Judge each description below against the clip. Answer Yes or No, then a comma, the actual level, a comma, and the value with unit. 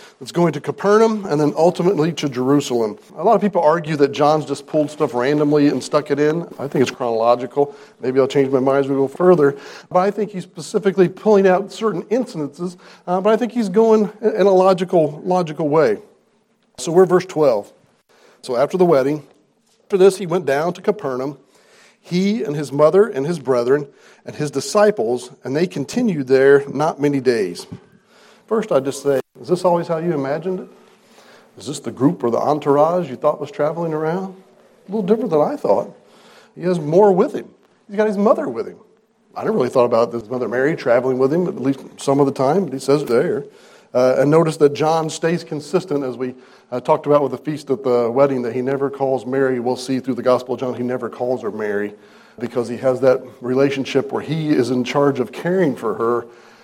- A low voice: No, medium, 150 Hz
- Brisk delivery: Yes, fast, 210 wpm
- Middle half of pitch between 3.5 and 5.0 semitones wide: No, wide, 5.5 semitones